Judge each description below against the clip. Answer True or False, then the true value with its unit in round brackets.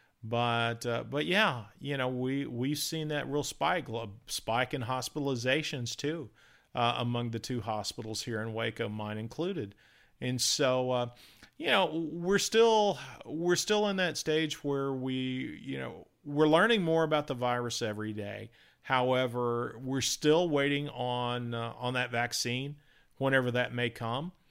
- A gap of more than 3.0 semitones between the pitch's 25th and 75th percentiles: True (4.1 semitones)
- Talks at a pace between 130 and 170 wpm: True (155 wpm)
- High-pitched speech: False (130 Hz)